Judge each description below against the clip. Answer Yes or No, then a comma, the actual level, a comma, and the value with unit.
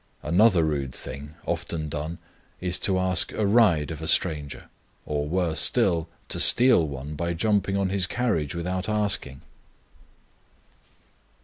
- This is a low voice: Yes, very low, 85 Hz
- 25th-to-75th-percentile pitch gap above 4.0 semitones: Yes, average, 4.4 semitones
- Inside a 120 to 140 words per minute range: Yes, slow, 135 wpm